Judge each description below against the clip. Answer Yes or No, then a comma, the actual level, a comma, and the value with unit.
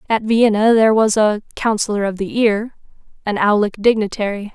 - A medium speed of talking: Yes, average, 145 wpm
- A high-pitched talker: Yes, high, 215 Hz